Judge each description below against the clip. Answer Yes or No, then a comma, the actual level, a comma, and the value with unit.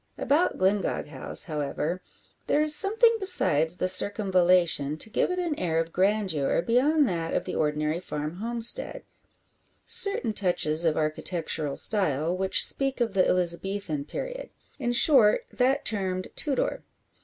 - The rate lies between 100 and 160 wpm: Yes, average, 140 wpm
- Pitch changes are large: Yes, wide, 7.4 semitones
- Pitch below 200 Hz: Yes, medium, 185 Hz